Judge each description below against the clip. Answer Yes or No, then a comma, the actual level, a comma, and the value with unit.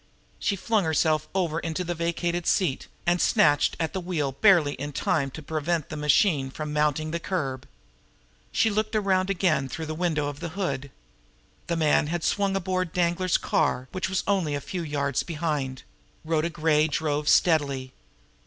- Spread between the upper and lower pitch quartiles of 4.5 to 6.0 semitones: No, average, 3.5 semitones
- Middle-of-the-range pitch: Yes, medium, 160 Hz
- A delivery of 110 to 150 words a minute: No, average, 170 wpm